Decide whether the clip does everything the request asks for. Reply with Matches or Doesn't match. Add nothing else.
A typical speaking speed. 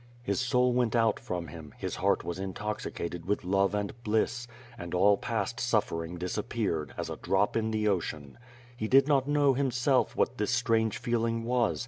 Matches